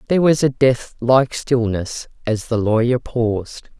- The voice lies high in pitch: No, low, 120 Hz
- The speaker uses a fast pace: No, average, 160 wpm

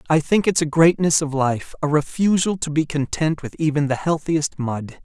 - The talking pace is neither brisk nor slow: Yes, average, 190 wpm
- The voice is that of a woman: No, male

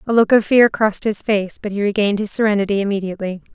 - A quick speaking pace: Yes, fast, 220 wpm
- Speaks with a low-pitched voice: No, high, 205 Hz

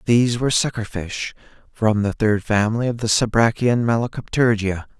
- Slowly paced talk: Yes, slow, 130 wpm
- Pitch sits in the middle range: No, low, 110 Hz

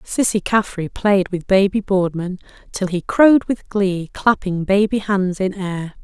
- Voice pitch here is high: Yes, high, 195 Hz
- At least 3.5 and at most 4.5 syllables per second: Yes, 4.1 syllables/s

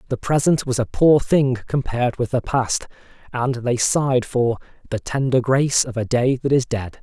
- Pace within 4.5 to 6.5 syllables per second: Yes, 4.9 syllables/s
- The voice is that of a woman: No, male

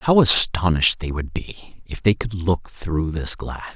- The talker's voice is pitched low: Yes, very low, 90 Hz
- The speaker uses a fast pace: No, average, 190 wpm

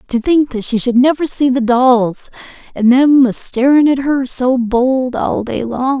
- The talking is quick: No, average, 190 wpm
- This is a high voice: Yes, very high, 255 Hz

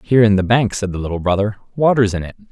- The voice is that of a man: Yes, male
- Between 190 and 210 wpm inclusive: No, fast, 260 wpm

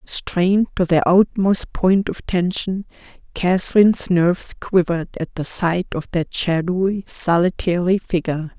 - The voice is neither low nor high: Yes, medium, 180 Hz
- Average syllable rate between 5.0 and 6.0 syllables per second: No, 4.5 syllables/s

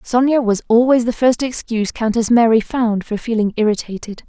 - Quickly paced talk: No, average, 170 wpm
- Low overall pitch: No, high, 230 Hz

